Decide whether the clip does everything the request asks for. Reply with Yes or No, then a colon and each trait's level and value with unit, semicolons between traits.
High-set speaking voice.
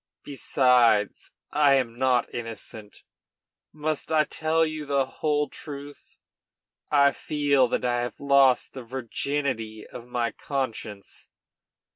No: low, 135 Hz